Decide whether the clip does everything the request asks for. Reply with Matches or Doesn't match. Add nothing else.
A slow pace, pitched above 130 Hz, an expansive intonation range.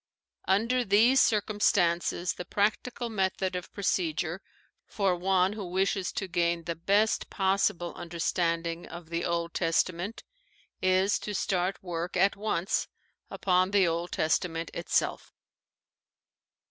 Doesn't match